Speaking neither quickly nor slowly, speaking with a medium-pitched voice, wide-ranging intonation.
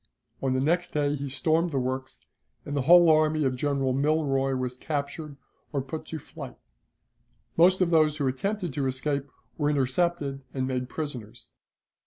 No: average, 165 wpm; medium, 145 Hz; average, 3.0 semitones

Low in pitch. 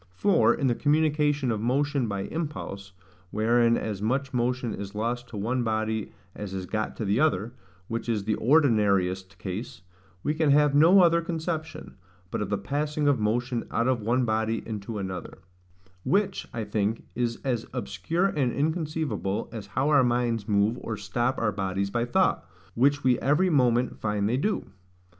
Yes: low, 120 Hz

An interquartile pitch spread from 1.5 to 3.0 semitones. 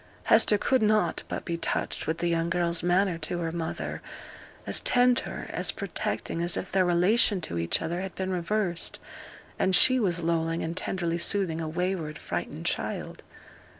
Yes: narrow, 2.5 semitones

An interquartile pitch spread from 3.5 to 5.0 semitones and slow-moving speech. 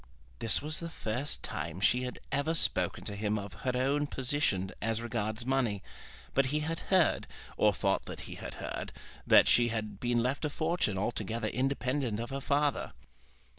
No: average, 4.7 semitones; average, 175 wpm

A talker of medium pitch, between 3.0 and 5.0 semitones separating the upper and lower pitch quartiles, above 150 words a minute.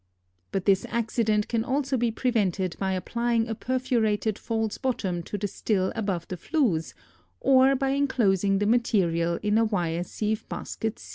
No: high, 215 Hz; average, 3.8 semitones; average, 160 wpm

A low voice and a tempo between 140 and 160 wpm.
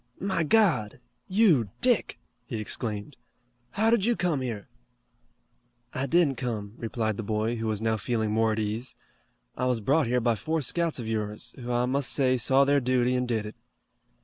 No: low, 125 Hz; average, 180 wpm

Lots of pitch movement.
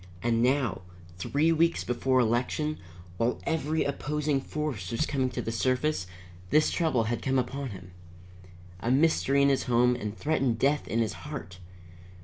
No: average, 4.4 semitones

